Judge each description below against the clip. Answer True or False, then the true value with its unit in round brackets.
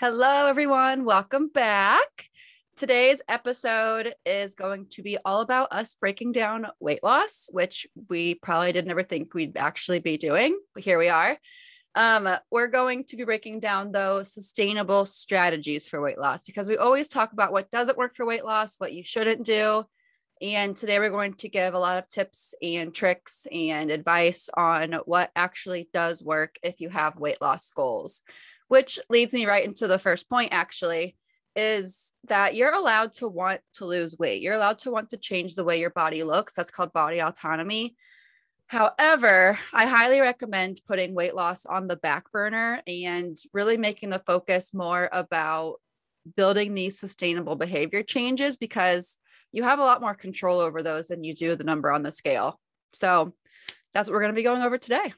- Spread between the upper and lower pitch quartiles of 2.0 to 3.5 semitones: False (4.8 semitones)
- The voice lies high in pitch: True (200 Hz)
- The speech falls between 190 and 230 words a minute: False (180 wpm)